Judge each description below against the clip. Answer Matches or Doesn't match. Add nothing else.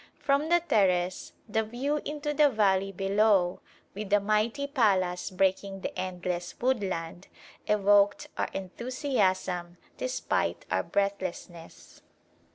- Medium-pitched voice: Doesn't match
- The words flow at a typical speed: Doesn't match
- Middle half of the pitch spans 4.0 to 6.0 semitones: Matches